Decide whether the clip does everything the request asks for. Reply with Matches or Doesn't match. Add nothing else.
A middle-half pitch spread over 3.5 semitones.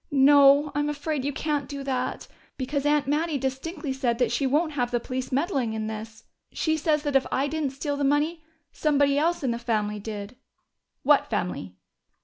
Doesn't match